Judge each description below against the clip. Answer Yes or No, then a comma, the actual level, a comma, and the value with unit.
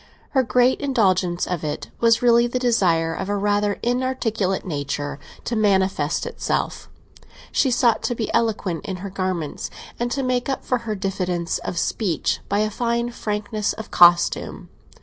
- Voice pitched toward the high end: Yes, high, 210 Hz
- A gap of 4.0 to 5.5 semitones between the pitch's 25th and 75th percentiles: Yes, average, 4.7 semitones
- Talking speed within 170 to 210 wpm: No, average, 160 wpm